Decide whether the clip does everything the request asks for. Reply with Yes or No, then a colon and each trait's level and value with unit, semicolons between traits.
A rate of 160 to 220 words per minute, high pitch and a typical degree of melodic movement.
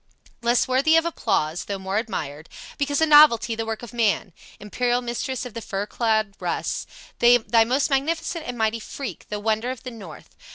Yes: average, 180 wpm; high, 235 Hz; average, 3.3 semitones